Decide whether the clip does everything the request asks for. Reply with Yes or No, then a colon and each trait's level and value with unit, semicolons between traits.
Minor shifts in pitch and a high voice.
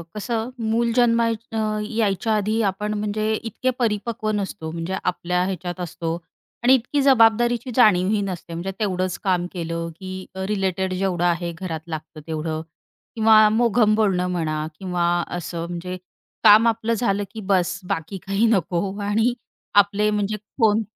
No: average, 3.7 semitones; high, 200 Hz